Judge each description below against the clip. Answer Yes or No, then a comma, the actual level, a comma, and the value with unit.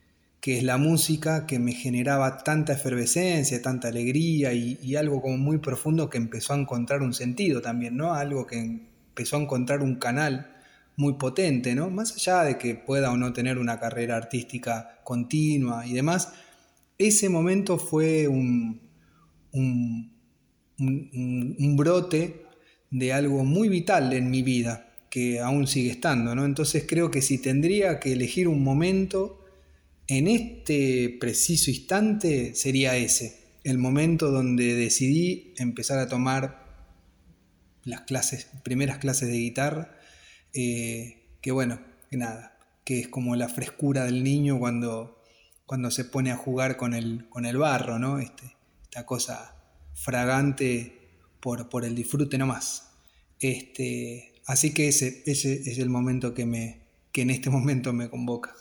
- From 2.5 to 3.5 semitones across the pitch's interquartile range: Yes, average, 2.9 semitones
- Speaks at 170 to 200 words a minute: No, average, 150 wpm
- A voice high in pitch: No, low, 130 Hz